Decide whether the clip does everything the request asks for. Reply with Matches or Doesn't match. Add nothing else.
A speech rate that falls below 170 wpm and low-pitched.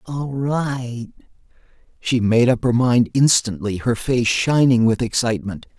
Matches